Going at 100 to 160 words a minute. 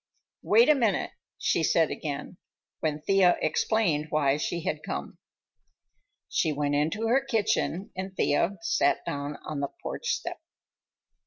Yes: average, 140 wpm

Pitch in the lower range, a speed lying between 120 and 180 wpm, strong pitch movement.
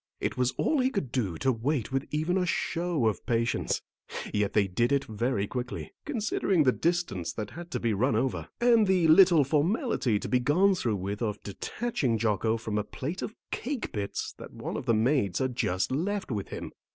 No: low, 130 Hz; average, 200 wpm; wide, 8.0 semitones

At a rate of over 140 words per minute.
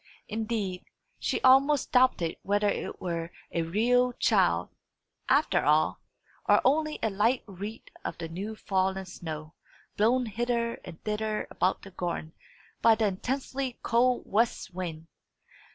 No: slow, 135 wpm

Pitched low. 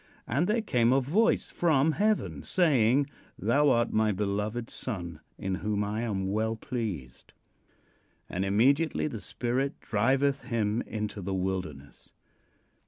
Yes: low, 115 Hz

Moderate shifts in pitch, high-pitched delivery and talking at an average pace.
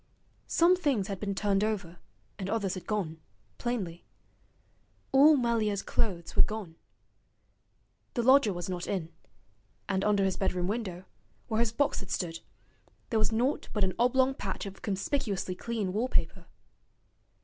Yes: average, 3.9 semitones; high, 205 Hz; average, 145 wpm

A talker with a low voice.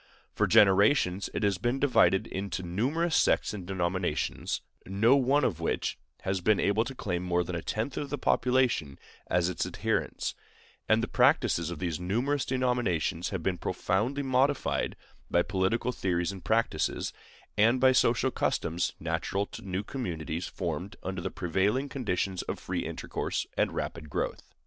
Yes: low, 100 Hz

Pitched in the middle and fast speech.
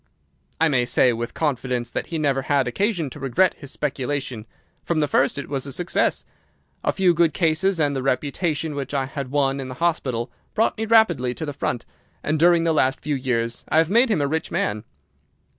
Yes: medium, 145 Hz; fast, 210 wpm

